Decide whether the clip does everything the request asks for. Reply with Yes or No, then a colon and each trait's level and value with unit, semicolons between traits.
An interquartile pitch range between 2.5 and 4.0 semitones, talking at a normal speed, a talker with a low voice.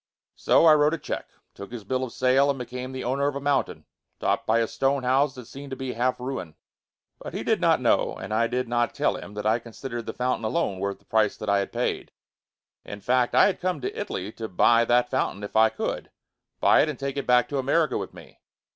No: average, 3.5 semitones; fast, 245 wpm; low, 125 Hz